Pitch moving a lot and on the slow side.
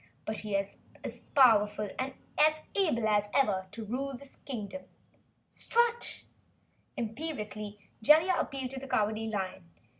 No: average, 4.7 semitones; slow, 125 wpm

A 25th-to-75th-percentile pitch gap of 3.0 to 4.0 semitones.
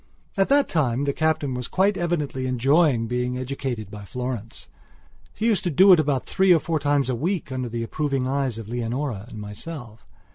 No: average, 4.7 semitones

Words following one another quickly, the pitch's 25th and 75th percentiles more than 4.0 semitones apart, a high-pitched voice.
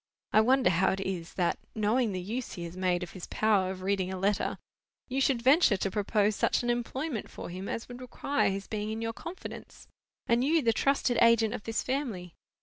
Yes: fast, 215 wpm; average, 4.5 semitones; high, 215 Hz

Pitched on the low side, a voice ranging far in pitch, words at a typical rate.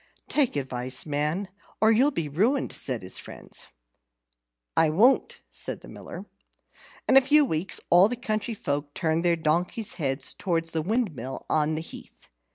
No: medium, 165 Hz; wide, 6.9 semitones; average, 160 wpm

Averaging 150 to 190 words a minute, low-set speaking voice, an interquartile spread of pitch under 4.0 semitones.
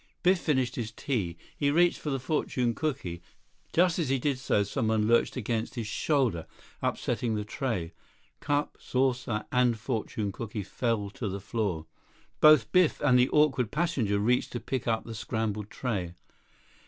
No: average, 160 wpm; low, 120 Hz; average, 4.3 semitones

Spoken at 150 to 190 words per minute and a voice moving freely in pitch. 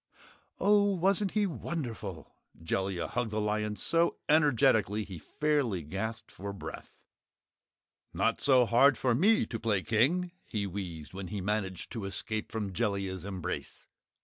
No: average, 140 wpm; wide, 6.5 semitones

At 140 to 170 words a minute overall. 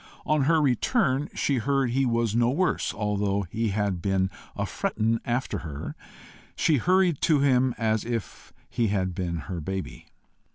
Yes: average, 160 wpm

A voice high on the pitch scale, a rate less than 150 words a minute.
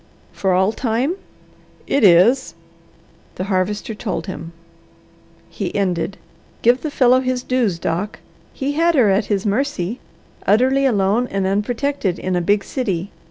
Yes: high, 210 Hz; average, 140 wpm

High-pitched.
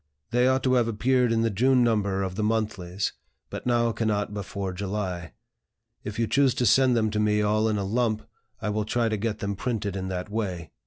No: low, 105 Hz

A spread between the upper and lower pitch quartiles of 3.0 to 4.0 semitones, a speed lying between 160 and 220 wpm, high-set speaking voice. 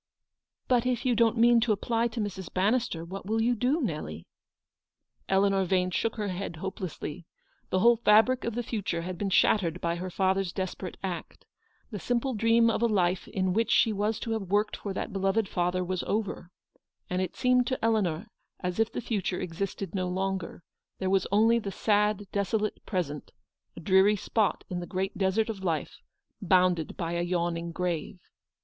Yes: average, 3.6 semitones; average, 190 wpm; high, 195 Hz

